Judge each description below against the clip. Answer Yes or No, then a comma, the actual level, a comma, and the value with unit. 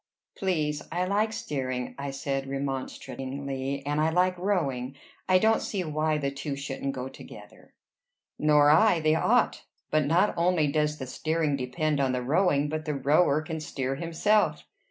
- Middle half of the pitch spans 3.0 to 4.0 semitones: Yes, average, 3.3 semitones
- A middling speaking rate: Yes, average, 160 wpm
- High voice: No, medium, 150 Hz